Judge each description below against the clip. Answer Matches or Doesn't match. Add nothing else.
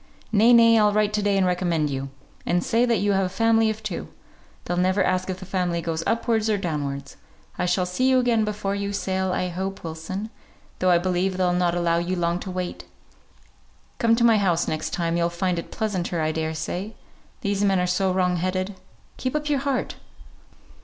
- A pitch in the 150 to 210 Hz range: Matches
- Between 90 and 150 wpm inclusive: Doesn't match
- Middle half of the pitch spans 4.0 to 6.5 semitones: Doesn't match